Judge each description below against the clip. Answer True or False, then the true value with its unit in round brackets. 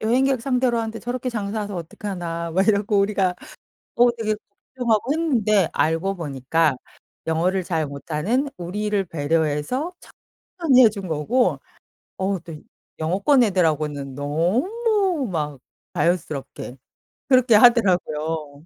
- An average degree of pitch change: False (6.8 semitones)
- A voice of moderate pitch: False (195 Hz)